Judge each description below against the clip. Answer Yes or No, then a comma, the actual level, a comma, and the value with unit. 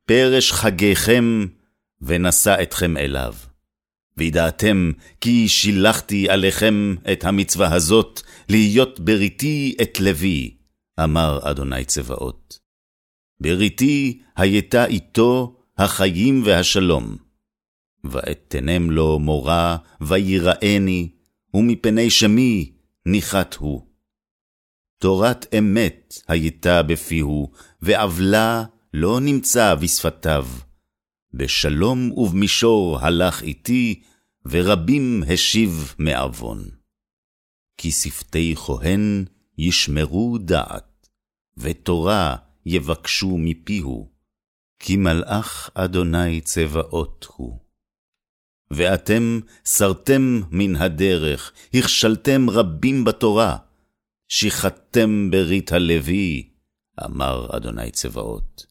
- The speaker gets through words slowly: Yes, slow, 75 wpm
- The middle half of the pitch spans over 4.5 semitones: Yes, wide, 5.6 semitones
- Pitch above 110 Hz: No, very low, 90 Hz